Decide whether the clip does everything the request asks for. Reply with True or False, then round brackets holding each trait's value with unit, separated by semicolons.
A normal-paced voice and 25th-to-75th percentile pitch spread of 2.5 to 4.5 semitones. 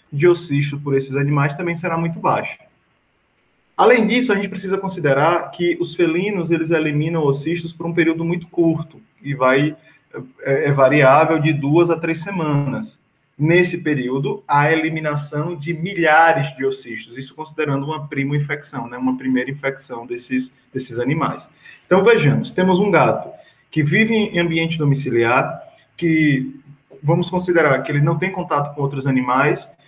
True (155 wpm; 3.5 semitones)